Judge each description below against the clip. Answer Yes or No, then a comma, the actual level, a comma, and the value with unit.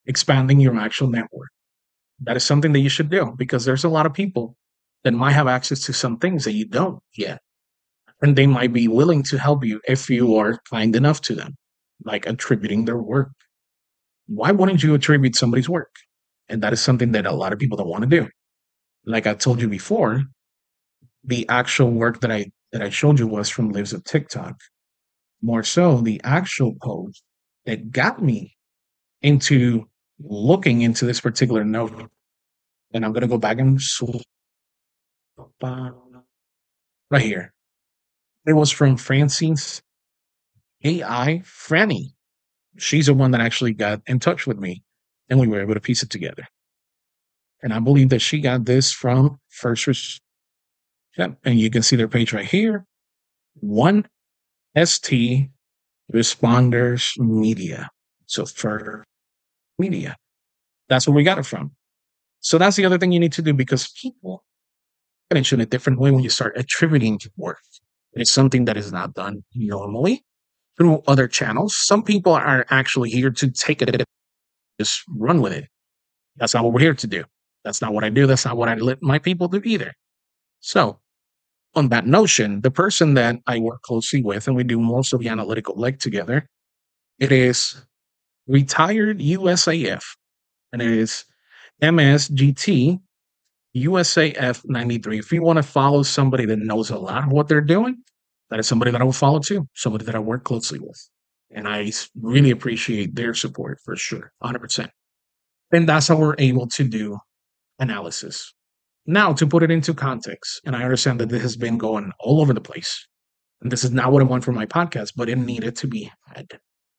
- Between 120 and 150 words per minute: No, average, 170 wpm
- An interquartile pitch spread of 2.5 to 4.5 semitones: Yes, average, 4.1 semitones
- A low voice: Yes, low, 125 Hz